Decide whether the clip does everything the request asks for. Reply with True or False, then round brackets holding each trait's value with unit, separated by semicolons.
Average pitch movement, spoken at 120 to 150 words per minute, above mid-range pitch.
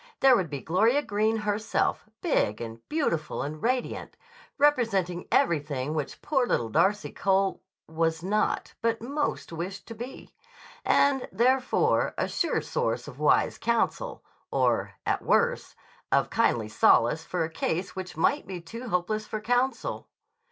False (6.9 semitones; 145 wpm; 205 Hz)